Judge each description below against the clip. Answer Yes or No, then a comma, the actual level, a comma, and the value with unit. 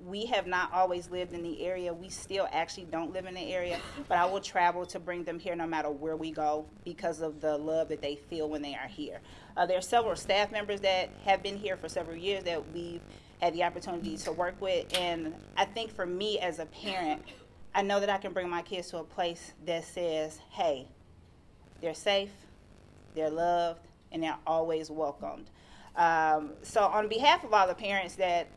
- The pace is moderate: No, fast, 210 wpm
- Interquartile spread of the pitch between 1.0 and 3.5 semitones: Yes, average, 2.9 semitones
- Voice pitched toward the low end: No, medium, 175 Hz